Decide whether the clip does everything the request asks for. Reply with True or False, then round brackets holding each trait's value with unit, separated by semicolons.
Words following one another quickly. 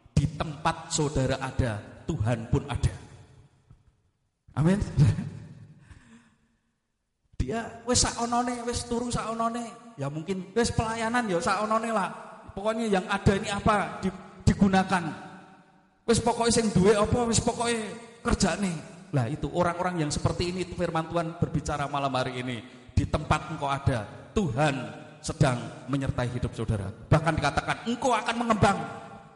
False (130 wpm)